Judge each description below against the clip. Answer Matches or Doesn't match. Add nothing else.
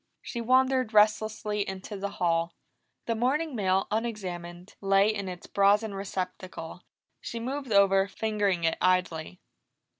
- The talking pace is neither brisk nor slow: Doesn't match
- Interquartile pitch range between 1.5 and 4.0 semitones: Matches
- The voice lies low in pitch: Doesn't match